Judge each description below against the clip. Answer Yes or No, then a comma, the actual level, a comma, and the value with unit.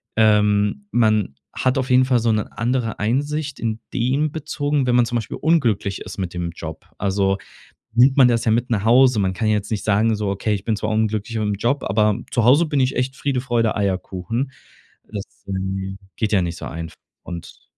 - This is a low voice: Yes, low, 110 Hz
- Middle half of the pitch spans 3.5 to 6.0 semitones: Yes, average, 4.2 semitones